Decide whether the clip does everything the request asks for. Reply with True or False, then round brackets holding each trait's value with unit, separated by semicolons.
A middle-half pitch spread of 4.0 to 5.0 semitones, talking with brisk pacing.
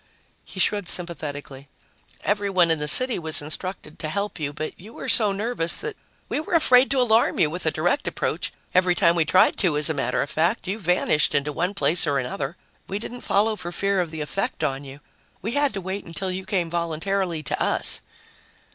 True (4.5 semitones; 210 wpm)